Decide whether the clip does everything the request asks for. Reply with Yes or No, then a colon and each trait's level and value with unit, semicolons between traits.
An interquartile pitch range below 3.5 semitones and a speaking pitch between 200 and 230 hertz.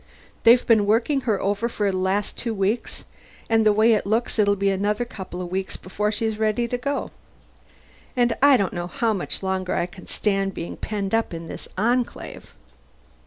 Yes: average, 3.0 semitones; high, 210 Hz